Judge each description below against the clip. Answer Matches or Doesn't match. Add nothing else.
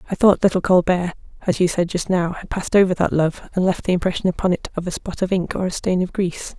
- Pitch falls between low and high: Matches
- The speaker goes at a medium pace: Doesn't match